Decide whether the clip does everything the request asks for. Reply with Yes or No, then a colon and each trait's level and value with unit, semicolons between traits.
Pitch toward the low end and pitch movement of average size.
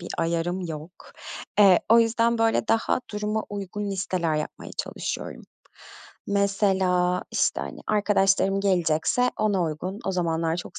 No: high, 190 Hz; average, 3.0 semitones